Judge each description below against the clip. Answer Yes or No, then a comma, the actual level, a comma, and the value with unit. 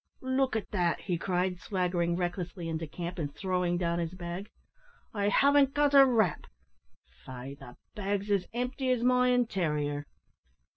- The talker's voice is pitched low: No, medium, 185 Hz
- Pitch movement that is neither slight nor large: No, wide, 5.8 semitones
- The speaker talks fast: No, average, 150 wpm